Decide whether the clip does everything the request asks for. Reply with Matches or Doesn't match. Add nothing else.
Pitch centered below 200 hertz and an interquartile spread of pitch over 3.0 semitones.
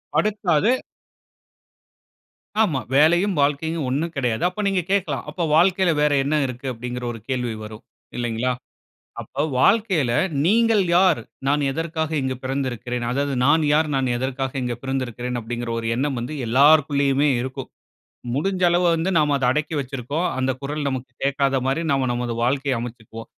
Matches